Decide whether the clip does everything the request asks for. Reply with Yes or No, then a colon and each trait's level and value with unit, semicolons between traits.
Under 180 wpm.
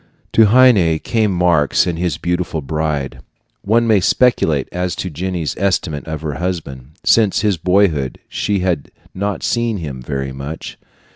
Yes: average, 150 wpm